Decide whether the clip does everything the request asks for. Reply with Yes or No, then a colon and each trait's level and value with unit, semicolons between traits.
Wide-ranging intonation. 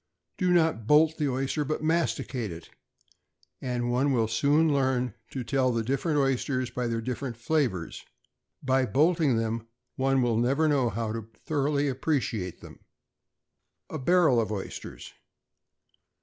No: average, 4.1 semitones